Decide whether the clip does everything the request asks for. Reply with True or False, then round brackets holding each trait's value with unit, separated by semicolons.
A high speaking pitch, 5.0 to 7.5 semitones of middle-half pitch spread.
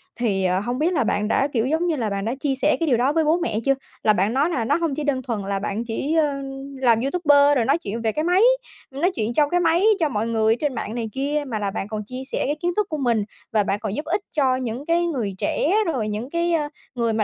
True (260 Hz; 5.5 semitones)